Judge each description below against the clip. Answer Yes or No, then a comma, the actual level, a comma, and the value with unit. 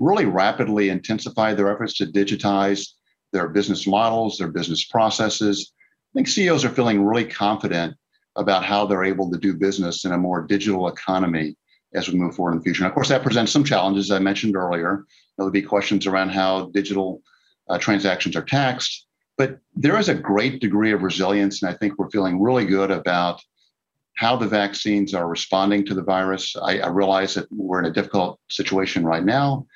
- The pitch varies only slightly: Yes, narrow, 1.6 semitones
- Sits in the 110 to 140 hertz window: No, low, 100 Hz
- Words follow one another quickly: No, average, 195 wpm